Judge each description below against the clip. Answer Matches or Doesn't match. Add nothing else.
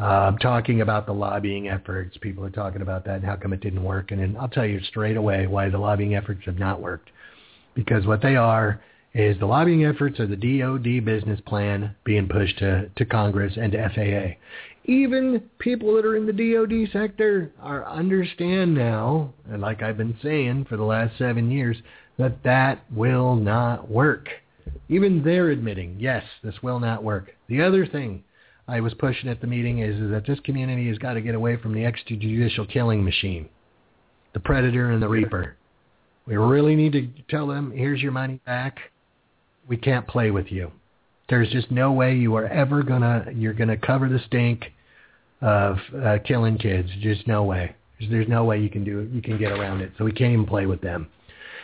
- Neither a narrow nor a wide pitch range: Matches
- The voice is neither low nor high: Doesn't match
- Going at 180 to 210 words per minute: Matches